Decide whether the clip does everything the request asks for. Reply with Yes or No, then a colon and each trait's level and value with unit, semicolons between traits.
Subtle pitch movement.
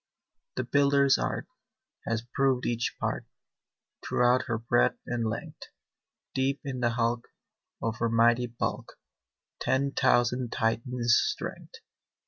Yes: narrow, 2.1 semitones